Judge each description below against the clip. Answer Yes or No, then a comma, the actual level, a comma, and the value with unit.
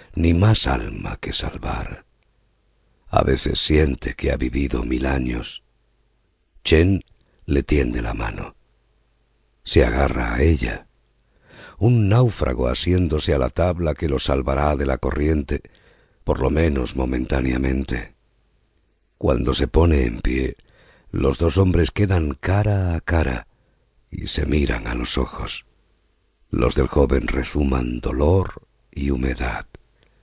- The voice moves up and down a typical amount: Yes, average, 4.8 semitones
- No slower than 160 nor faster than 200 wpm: No, slow, 125 wpm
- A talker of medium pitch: No, very low, 75 Hz